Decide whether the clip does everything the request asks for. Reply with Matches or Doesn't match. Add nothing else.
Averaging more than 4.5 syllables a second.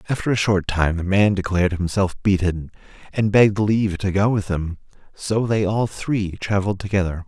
Matches